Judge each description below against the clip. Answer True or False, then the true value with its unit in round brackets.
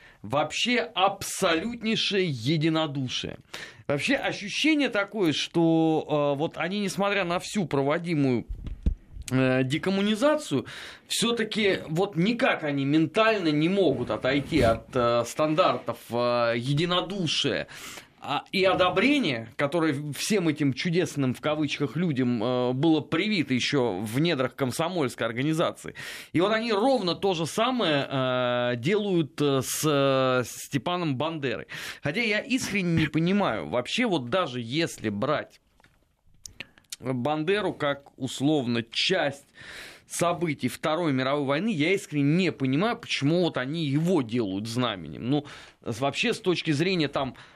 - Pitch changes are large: True (6.0 semitones)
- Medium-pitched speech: True (155 Hz)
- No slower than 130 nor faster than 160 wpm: False (110 wpm)